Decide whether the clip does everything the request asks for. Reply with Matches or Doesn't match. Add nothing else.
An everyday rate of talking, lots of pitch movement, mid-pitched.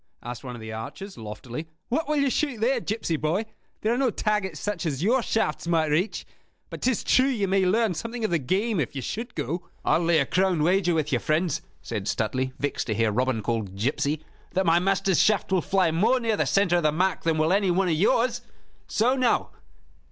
Doesn't match